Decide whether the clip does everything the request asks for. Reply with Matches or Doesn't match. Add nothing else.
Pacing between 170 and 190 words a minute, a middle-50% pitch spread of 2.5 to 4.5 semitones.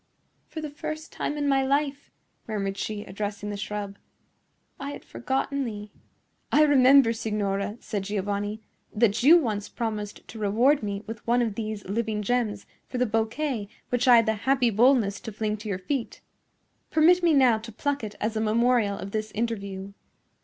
Matches